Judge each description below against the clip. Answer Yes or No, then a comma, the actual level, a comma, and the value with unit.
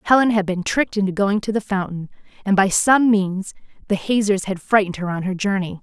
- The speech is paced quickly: Yes, fast, 215 wpm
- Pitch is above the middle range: Yes, high, 200 Hz